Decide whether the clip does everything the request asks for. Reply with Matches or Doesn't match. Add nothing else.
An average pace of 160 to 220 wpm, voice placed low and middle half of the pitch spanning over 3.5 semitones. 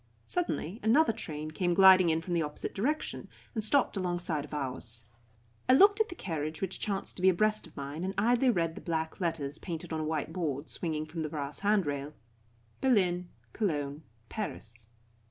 Doesn't match